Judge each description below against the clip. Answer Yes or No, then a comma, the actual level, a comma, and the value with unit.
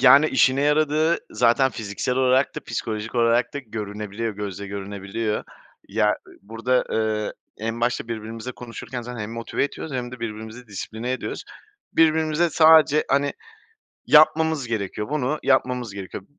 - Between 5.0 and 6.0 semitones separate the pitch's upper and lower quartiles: No, average, 4.2 semitones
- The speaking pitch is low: Yes, low, 120 Hz